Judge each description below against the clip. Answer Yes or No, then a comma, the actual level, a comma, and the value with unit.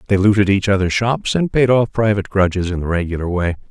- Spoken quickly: Yes, fast, 225 wpm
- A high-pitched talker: No, low, 100 Hz